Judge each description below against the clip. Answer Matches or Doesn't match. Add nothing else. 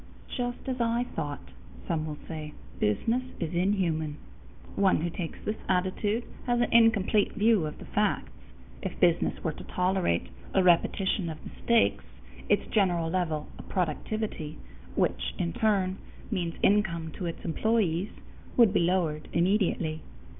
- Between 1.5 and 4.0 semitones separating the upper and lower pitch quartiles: Doesn't match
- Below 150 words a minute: Matches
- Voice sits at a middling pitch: Matches